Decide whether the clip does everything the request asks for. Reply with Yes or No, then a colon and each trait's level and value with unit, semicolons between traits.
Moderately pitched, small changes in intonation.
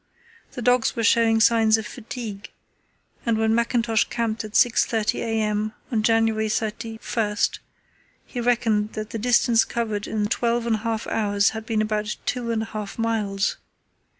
No: high, 225 Hz; narrow, 1.4 semitones